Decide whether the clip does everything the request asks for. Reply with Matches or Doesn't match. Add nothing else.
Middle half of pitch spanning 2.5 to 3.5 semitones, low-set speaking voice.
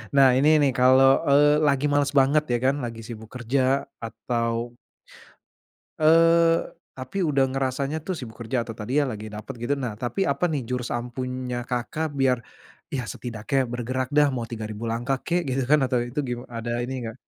Matches